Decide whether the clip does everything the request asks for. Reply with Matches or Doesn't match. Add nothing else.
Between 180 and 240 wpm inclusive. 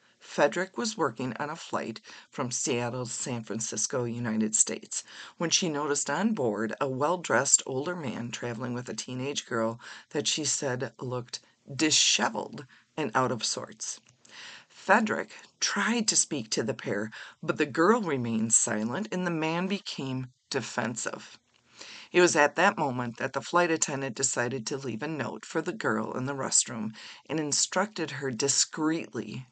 Doesn't match